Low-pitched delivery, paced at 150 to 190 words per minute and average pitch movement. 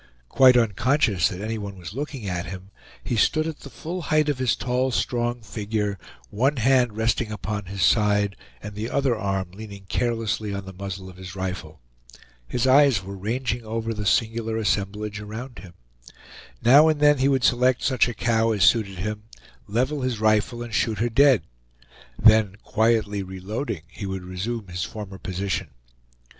Yes: low, 110 Hz; average, 175 wpm; average, 3.8 semitones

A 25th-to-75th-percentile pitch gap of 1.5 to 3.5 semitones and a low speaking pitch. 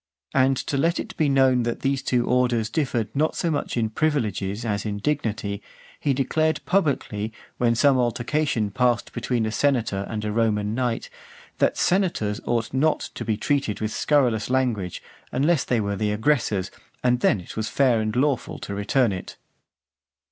No: average, 4.3 semitones; low, 120 Hz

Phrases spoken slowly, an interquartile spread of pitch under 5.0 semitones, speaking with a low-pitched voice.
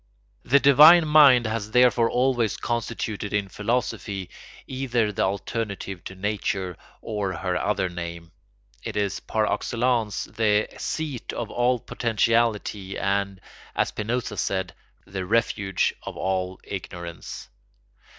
Yes: slow, 120 wpm; average, 3.6 semitones; low, 105 Hz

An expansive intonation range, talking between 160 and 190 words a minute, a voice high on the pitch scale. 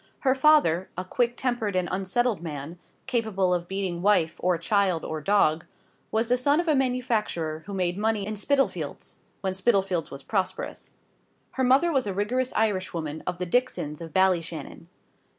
Yes: wide, 5.9 semitones; average, 165 wpm; high, 195 Hz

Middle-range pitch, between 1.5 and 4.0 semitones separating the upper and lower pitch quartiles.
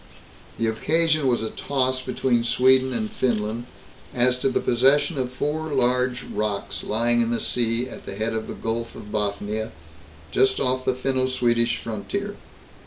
No: low, 125 Hz; narrow, 2.4 semitones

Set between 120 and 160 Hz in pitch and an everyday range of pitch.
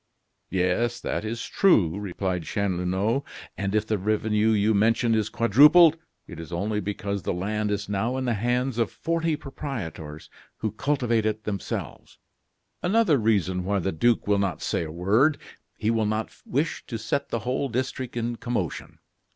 No: low, 110 Hz; average, 3.5 semitones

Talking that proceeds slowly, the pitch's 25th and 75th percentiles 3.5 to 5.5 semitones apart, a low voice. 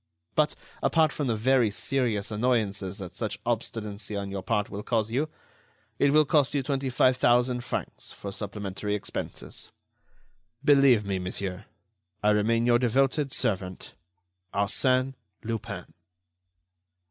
Yes: slow, 130 wpm; average, 4.3 semitones; low, 115 Hz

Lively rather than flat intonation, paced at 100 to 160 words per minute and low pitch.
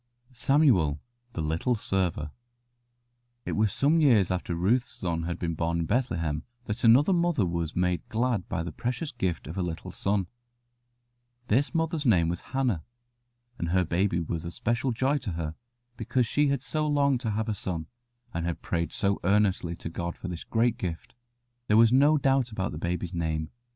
No: wide, 6.7 semitones; average, 180 wpm; low, 100 Hz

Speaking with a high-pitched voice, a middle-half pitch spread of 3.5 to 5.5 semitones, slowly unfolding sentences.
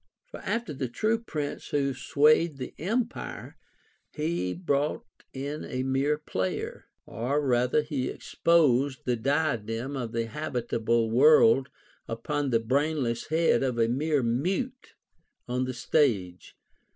No: low, 135 Hz; average, 4.2 semitones; slow, 125 wpm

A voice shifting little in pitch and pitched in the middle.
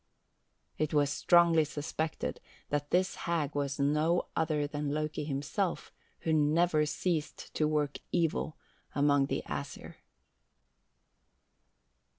Yes: narrow, 1.9 semitones; medium, 150 Hz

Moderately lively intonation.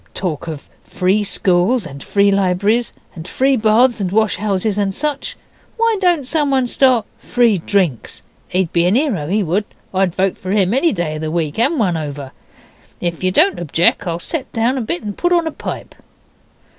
No: wide, 6.0 semitones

